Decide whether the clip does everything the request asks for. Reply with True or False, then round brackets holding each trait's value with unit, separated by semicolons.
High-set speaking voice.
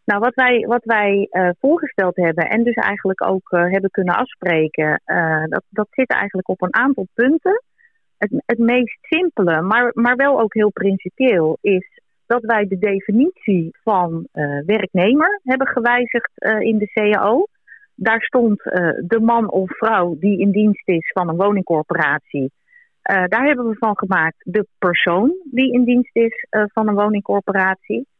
True (210 Hz)